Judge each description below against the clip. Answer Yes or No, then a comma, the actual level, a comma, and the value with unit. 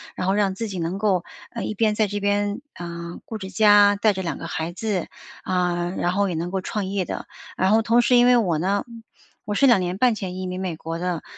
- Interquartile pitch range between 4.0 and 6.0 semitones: No, average, 2.9 semitones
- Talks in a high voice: Yes, high, 195 Hz